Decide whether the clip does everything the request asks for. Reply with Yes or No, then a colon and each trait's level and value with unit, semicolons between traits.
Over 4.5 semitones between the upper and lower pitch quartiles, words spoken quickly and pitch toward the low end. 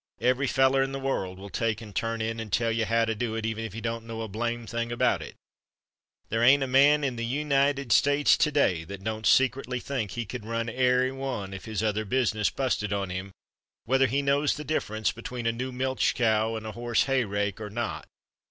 No: average, 3.3 semitones; fast, 225 wpm; low, 115 Hz